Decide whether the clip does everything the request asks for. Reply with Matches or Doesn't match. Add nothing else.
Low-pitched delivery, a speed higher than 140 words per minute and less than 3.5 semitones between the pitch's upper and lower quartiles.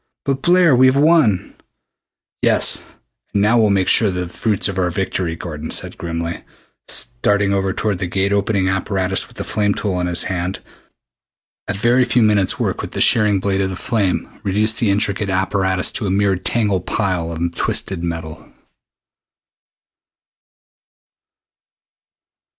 Matches